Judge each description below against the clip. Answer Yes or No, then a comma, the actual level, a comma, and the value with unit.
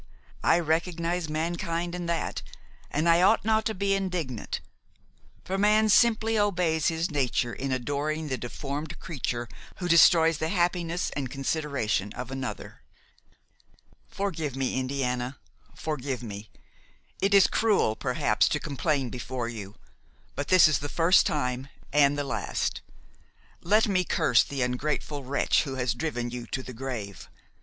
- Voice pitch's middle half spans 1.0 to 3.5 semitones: No, average, 5.2 semitones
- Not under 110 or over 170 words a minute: Yes, average, 145 wpm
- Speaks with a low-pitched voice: No, medium, 150 Hz